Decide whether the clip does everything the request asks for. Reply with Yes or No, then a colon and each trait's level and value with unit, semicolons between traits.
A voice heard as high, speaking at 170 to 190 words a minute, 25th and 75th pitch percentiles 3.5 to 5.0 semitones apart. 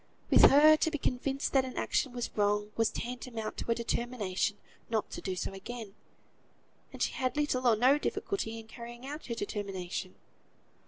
Yes: high, 235 Hz; average, 175 wpm; average, 3.8 semitones